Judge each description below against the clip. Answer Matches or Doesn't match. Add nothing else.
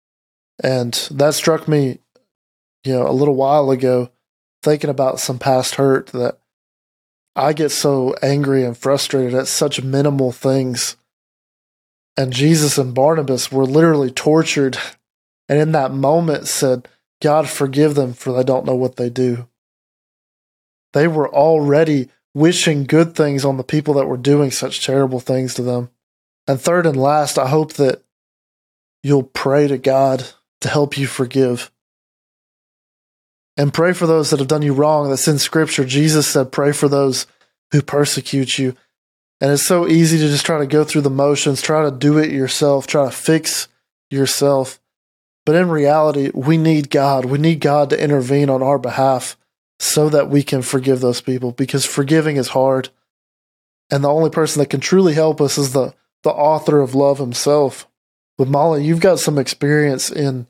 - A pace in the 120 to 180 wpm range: Matches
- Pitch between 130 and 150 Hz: Matches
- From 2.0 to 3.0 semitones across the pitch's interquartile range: Matches